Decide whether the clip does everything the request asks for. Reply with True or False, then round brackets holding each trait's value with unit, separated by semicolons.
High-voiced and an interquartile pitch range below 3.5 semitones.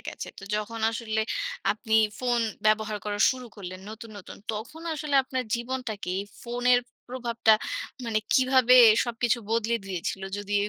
True (230 Hz; 2.8 semitones)